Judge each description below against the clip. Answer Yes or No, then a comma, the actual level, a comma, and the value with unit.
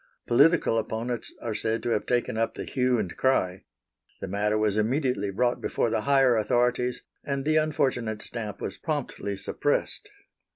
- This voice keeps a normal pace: Yes, average, 160 wpm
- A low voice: Yes, low, 120 Hz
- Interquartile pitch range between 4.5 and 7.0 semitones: No, average, 3.7 semitones